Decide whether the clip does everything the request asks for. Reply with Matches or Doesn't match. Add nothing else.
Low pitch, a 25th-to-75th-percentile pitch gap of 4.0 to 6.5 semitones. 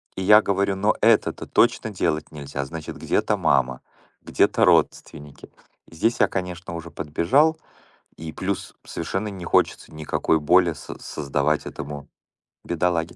Matches